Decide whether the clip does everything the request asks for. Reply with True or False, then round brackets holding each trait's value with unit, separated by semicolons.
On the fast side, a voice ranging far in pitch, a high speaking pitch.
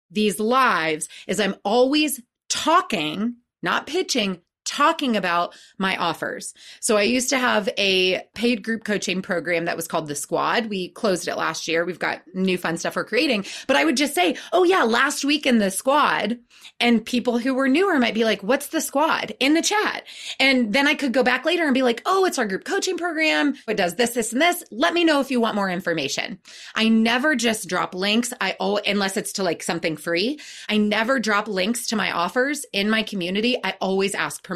True (210 wpm; 6.2 semitones; 230 Hz)